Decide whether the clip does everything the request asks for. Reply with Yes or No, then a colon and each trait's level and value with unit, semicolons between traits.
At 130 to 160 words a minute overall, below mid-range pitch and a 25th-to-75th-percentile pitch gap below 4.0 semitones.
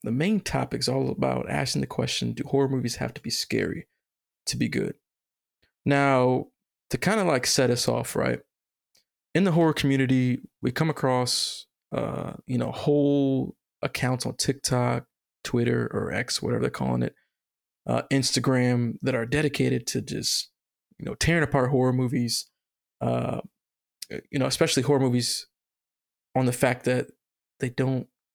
Yes: average, 155 wpm; low, 130 Hz; narrow, 2.4 semitones